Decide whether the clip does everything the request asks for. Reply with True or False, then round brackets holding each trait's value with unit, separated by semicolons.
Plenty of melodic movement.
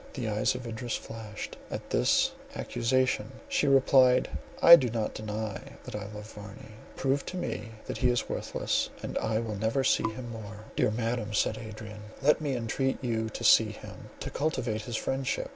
False (3.1 semitones)